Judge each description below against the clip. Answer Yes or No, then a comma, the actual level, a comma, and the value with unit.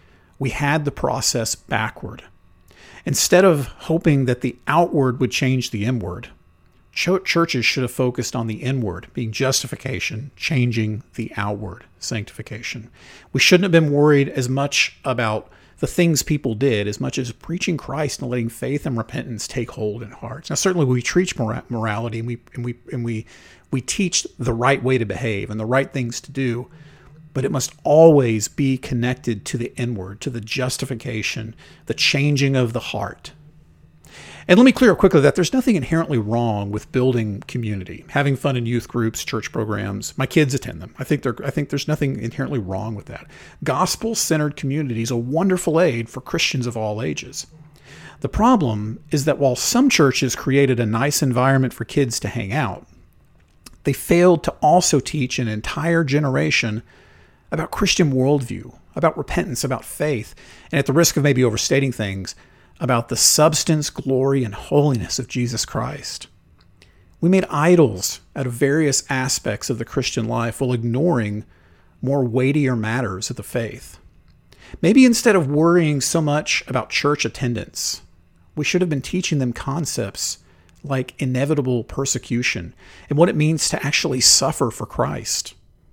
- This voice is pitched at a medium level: No, low, 130 Hz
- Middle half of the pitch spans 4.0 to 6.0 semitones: Yes, average, 4.5 semitones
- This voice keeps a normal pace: Yes, average, 165 wpm